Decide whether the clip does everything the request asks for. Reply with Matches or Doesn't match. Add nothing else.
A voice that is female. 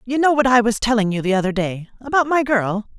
Matches